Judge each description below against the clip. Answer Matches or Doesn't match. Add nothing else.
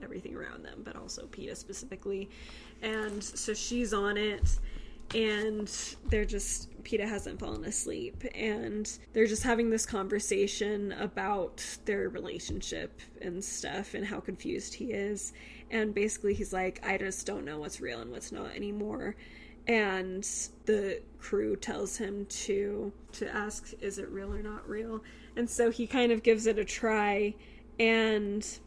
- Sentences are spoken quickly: Doesn't match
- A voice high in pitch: Matches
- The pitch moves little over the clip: Matches